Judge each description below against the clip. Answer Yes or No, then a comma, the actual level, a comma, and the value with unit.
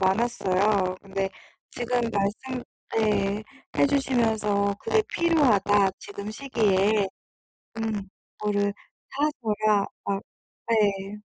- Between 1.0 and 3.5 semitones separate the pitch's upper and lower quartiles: Yes, narrow, 2.6 semitones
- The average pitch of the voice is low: No, high, 210 Hz